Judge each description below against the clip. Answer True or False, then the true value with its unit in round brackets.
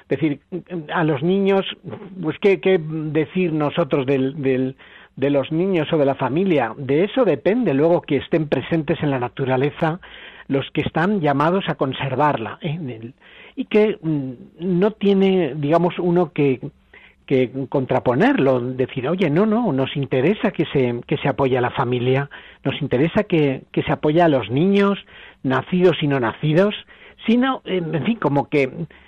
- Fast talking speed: False (160 wpm)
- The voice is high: False (155 Hz)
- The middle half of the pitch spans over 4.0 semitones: True (4.9 semitones)